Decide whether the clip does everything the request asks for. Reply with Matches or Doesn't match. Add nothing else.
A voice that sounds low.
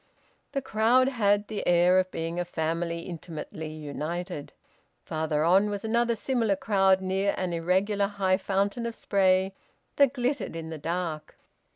Doesn't match